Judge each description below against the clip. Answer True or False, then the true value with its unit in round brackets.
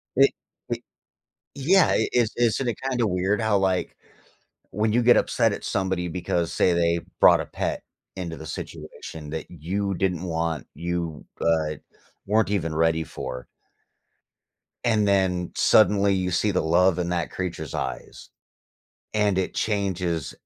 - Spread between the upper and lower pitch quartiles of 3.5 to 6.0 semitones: True (3.8 semitones)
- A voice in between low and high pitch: False (90 Hz)